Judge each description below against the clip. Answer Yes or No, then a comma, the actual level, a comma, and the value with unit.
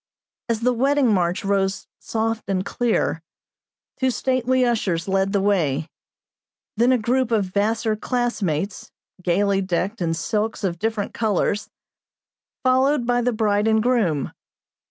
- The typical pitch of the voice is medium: No, high, 215 Hz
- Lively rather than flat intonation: No, average, 4.0 semitones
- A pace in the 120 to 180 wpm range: Yes, slow, 135 wpm